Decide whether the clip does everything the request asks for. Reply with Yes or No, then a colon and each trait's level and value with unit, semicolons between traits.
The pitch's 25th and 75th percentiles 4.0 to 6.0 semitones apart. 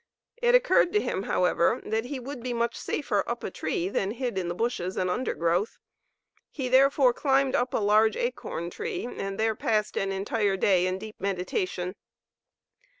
Yes: average, 5.2 semitones